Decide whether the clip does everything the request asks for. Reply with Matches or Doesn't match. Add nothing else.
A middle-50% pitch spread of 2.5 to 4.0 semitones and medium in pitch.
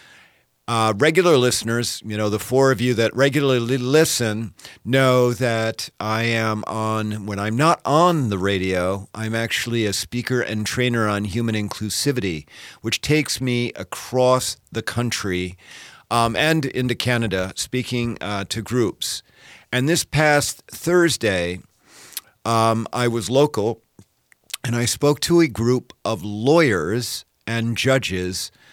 Doesn't match